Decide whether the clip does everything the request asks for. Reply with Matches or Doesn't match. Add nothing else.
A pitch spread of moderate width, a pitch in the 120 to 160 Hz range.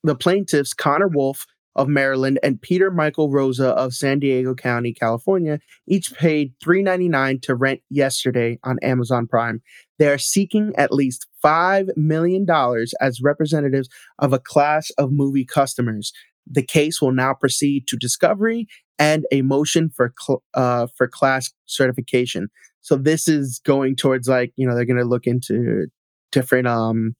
Matches